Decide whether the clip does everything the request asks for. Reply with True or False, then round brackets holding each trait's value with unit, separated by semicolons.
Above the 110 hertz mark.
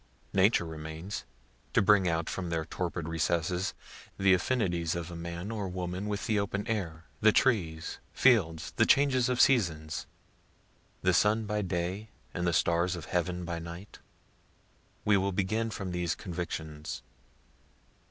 False (90 Hz)